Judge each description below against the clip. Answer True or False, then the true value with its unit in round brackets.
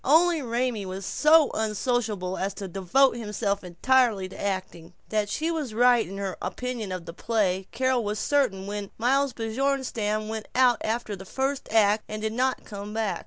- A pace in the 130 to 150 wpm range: False (175 wpm)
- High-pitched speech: True (220 Hz)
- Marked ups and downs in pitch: False (4.2 semitones)